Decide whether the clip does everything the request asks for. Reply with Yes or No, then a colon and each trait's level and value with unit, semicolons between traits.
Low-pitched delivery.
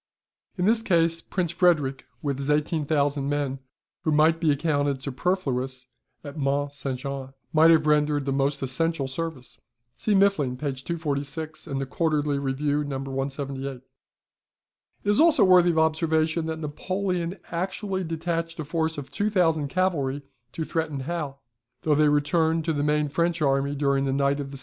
No: medium, 150 Hz